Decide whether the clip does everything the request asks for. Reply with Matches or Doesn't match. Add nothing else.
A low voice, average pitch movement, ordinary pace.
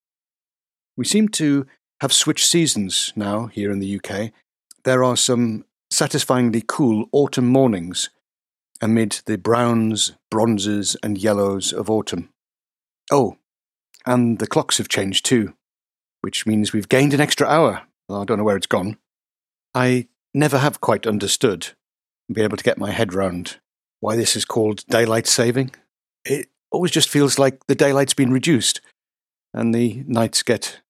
Matches